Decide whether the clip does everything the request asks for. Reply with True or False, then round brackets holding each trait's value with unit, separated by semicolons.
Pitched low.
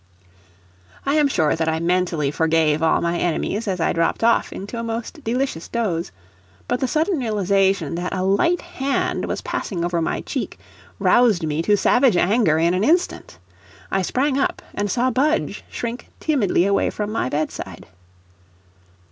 False (200 Hz)